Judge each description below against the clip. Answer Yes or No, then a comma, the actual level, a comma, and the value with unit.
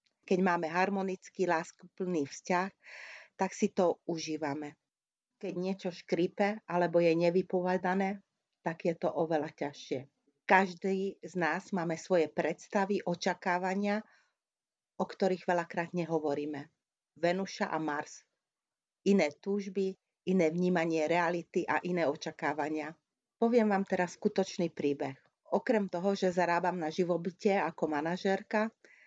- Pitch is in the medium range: Yes, medium, 180 Hz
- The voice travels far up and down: No, average, 2.8 semitones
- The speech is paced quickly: No, average, 115 wpm